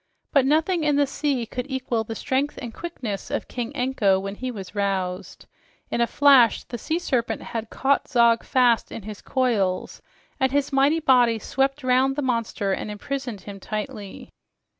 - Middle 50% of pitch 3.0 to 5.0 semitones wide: Yes, average, 4.3 semitones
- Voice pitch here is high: Yes, very high, 250 Hz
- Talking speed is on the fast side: No, average, 175 wpm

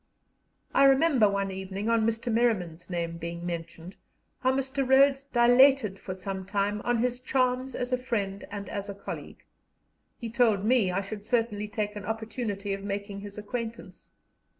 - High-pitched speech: Yes, high, 210 Hz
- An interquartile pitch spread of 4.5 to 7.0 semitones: No, average, 3.9 semitones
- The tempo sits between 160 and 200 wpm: Yes, average, 165 wpm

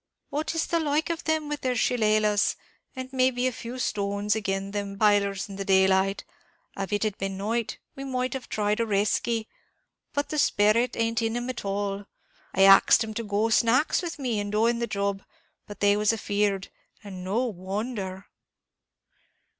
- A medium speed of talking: Yes, average, 185 wpm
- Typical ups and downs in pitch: Yes, average, 3.8 semitones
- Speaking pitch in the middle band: No, high, 215 Hz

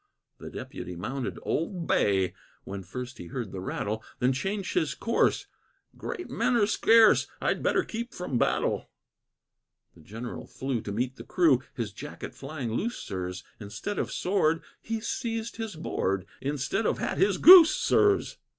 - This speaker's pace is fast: No, average, 160 wpm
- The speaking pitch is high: No, low, 135 Hz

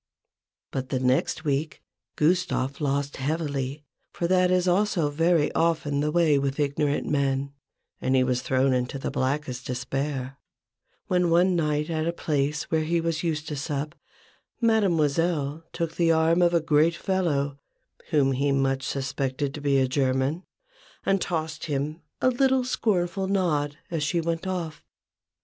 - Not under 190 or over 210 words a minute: No, average, 155 wpm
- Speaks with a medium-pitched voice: Yes, medium, 150 Hz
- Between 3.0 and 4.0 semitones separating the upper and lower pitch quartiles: Yes, average, 3.6 semitones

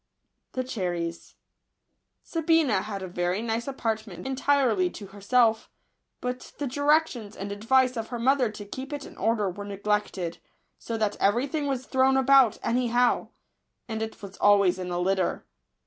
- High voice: Yes, high, 225 Hz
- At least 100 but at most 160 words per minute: Yes, average, 155 wpm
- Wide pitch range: No, average, 4.6 semitones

